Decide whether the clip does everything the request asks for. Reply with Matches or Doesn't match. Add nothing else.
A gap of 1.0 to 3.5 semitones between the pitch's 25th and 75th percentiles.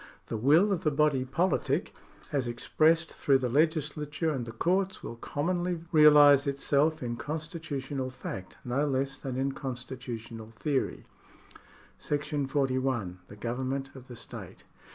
Matches